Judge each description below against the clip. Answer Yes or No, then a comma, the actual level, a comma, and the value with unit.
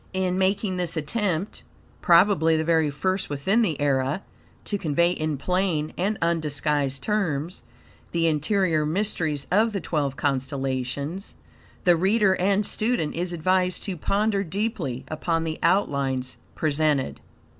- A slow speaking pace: Yes, slow, 130 wpm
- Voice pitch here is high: No, medium, 165 Hz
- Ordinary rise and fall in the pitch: Yes, average, 4.5 semitones